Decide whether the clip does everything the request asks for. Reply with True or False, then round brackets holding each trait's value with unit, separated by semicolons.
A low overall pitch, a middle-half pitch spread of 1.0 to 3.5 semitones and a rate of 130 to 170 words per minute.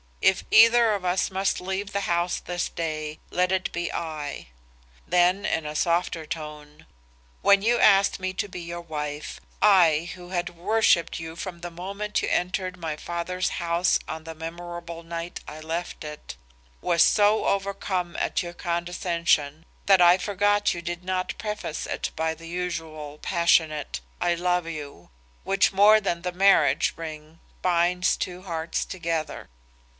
False (175 Hz; 2.4 semitones; 155 wpm)